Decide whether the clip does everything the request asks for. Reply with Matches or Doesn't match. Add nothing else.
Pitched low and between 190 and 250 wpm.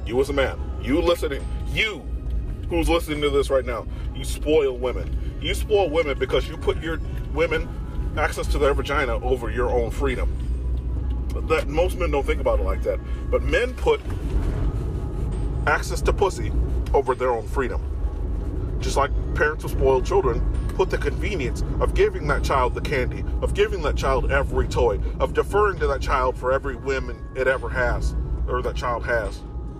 Doesn't match